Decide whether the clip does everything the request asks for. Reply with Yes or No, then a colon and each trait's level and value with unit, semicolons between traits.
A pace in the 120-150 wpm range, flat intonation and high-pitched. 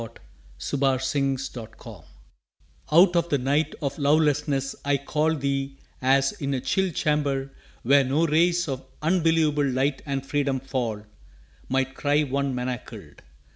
No: average, 145 wpm; narrow, 2.0 semitones; medium, 140 Hz